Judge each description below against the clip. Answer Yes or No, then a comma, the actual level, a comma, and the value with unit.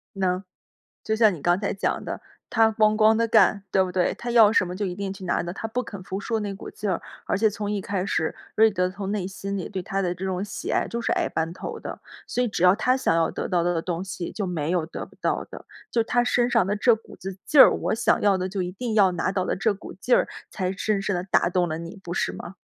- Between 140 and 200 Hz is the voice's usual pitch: Yes, high, 195 Hz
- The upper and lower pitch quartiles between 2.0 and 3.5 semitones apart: Yes, average, 3.0 semitones